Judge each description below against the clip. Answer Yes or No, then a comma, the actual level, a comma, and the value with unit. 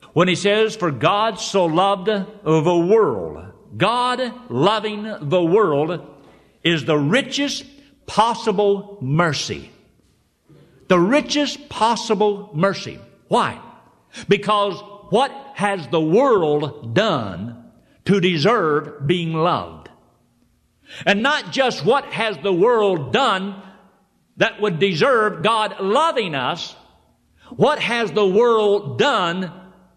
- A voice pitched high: Yes, high, 200 Hz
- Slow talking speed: Yes, slow, 105 wpm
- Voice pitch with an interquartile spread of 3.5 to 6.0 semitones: Yes, average, 4.0 semitones